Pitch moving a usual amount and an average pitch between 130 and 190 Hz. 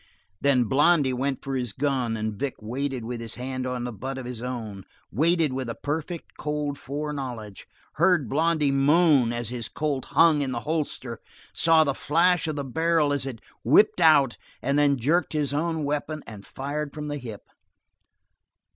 Yes: average, 3.5 semitones; medium, 140 Hz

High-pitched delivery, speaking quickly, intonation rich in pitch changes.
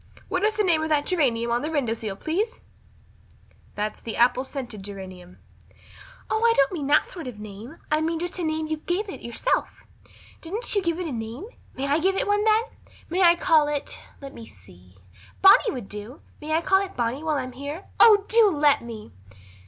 Yes: very high, 300 Hz; fast, 210 wpm; wide, 7.6 semitones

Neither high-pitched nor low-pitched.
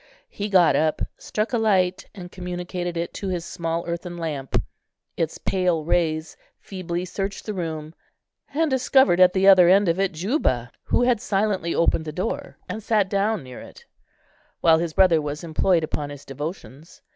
Yes: medium, 175 Hz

